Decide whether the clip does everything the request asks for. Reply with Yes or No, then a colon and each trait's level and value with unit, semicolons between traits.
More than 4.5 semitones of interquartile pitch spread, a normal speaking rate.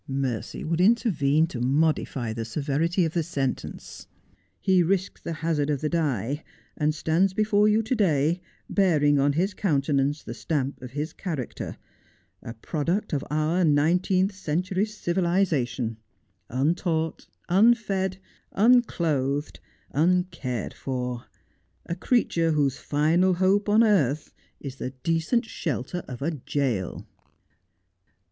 No: average, 4.9 semitones; slow, 125 wpm